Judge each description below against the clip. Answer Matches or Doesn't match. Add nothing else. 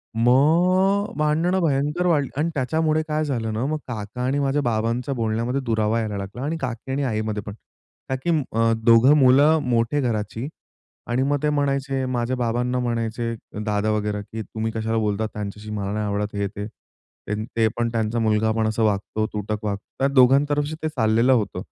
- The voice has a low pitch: Matches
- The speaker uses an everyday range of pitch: Matches